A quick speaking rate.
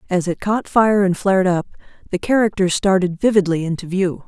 No: average, 185 wpm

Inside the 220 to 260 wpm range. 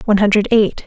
No: fast, 210 wpm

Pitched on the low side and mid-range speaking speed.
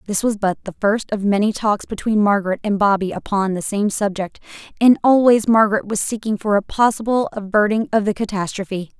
No: high, 205 Hz; average, 185 wpm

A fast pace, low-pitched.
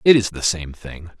Yes: fast, 250 wpm; very low, 95 Hz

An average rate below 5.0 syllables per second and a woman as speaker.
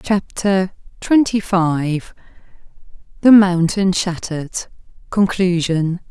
Yes: 3.3 syllables/s; female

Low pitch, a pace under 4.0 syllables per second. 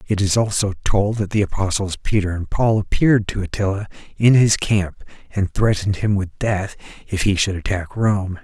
No: low, 100 Hz; 5.1 syllables/s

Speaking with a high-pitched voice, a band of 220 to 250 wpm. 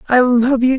Yes: very high, 250 Hz; fast, 230 wpm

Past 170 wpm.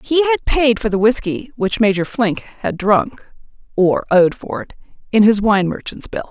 Yes: average, 190 wpm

